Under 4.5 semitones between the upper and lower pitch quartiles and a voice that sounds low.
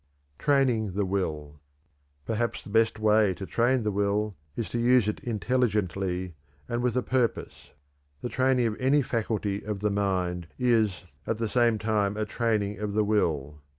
Yes: average, 3.1 semitones; low, 105 Hz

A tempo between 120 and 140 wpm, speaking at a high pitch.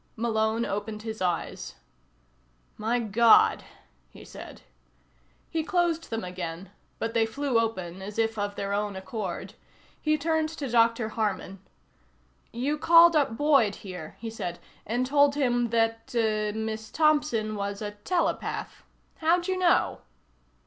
Yes: slow, 135 wpm; high, 225 Hz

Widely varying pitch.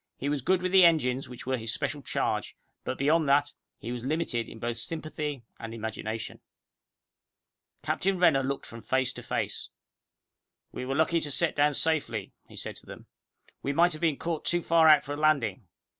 No: average, 4.2 semitones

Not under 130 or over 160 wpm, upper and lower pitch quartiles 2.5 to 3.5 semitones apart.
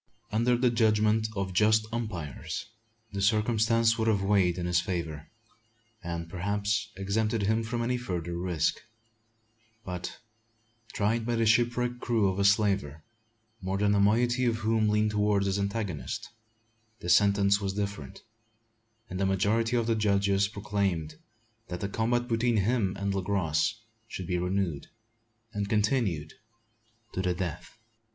Yes: average, 145 wpm; average, 3.0 semitones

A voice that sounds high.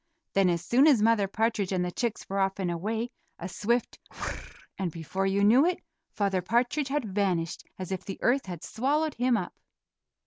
Yes: high, 200 Hz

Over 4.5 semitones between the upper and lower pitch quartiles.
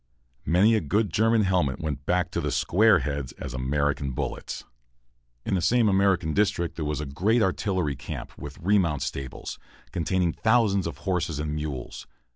Yes: average, 5.2 semitones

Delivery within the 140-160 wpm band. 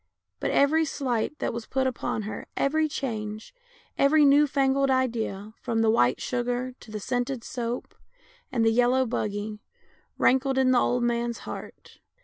Yes: average, 155 wpm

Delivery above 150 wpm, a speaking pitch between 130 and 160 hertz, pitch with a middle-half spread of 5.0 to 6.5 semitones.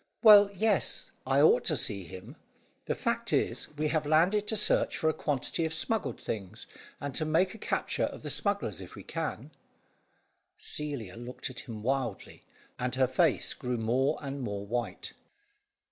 Yes: average, 170 wpm; low, 135 Hz; wide, 5.4 semitones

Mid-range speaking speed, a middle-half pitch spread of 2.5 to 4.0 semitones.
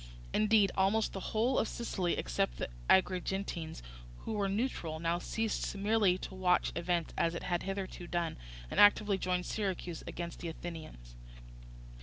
Yes: average, 150 wpm; average, 3.2 semitones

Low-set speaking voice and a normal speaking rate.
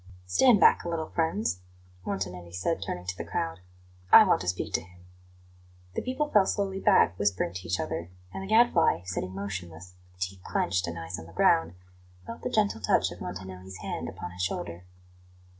Yes: very low, 90 Hz; average, 190 wpm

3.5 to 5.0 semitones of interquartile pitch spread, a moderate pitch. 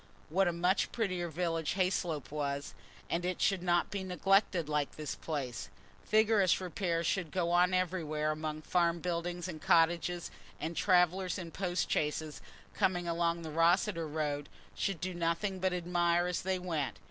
No: narrow, 2.4 semitones; medium, 175 Hz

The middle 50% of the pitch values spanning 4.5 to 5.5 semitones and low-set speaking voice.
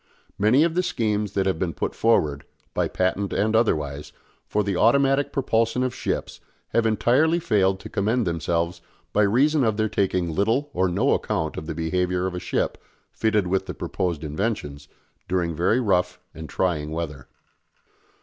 Yes: average, 5.1 semitones; very low, 95 Hz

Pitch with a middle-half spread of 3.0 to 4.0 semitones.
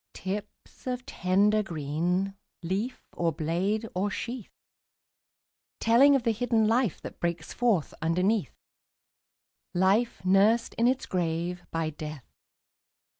No: average, 5.0 semitones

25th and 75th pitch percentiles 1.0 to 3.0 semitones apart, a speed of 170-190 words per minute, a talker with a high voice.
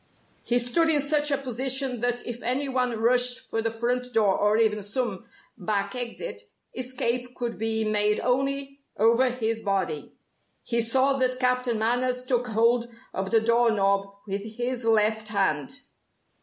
No: narrow, 2.5 semitones; average, 155 wpm; high, 240 Hz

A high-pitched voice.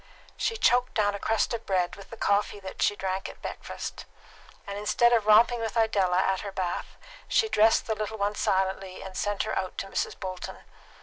Yes: high, 205 Hz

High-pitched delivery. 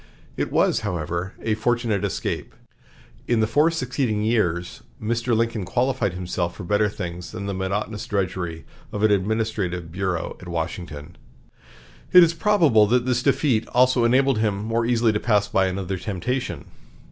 No: low, 105 Hz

